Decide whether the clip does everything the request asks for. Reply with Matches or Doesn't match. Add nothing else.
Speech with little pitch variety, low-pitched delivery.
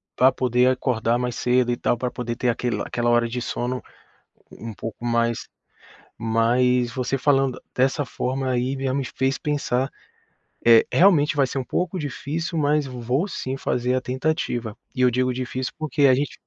Matches